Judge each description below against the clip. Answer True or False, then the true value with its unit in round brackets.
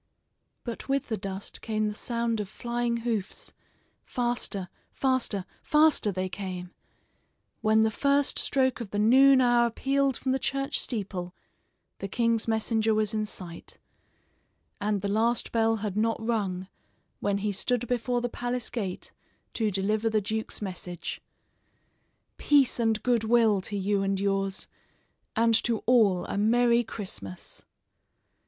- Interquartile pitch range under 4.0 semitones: True (3.3 semitones)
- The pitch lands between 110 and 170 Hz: False (220 Hz)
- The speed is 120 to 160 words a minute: True (140 wpm)